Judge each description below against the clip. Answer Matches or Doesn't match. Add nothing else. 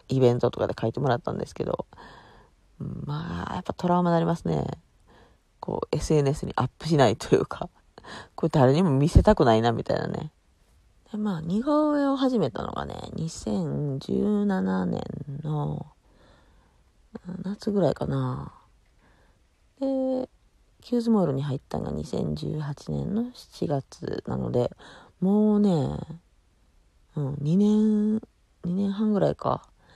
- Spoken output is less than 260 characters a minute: Matches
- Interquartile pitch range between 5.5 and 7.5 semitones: Doesn't match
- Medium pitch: Matches